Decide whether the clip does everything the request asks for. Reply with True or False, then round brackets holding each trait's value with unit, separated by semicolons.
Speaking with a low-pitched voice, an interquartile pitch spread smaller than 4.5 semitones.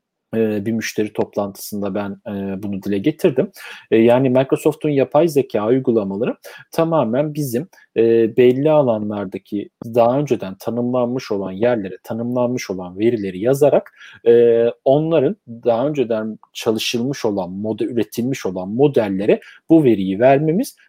True (115 Hz; 4.1 semitones)